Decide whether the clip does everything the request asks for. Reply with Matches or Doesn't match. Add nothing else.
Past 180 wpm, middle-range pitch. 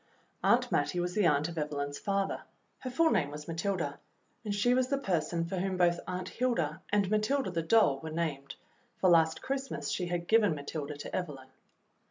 Matches